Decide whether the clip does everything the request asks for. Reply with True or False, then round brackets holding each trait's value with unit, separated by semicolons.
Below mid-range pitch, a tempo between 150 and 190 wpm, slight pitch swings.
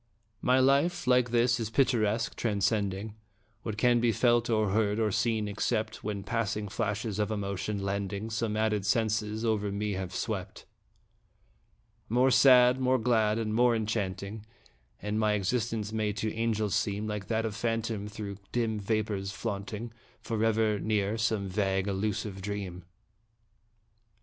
False (110 Hz; 140 wpm; 2.0 semitones)